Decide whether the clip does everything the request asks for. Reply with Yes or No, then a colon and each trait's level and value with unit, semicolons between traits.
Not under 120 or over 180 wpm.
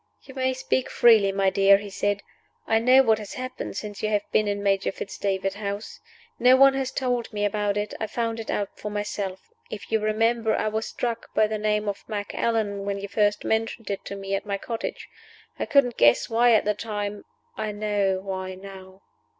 No: fast, 205 wpm